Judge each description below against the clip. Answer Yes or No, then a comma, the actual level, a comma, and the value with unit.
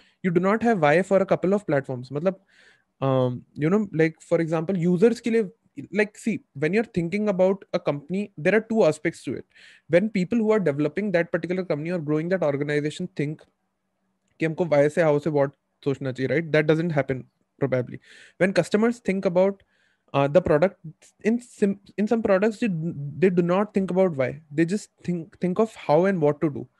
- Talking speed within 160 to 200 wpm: Yes, average, 195 wpm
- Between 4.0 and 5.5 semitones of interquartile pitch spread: Yes, average, 4.7 semitones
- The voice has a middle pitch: Yes, medium, 180 Hz